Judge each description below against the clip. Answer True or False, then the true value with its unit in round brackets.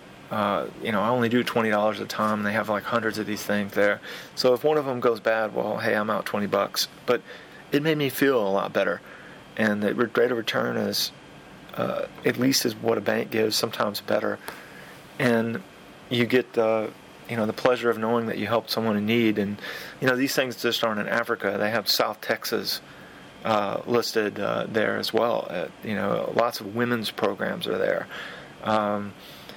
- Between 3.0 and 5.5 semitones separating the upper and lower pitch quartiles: False (2.4 semitones)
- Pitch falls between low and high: False (115 Hz)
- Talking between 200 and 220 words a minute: True (205 wpm)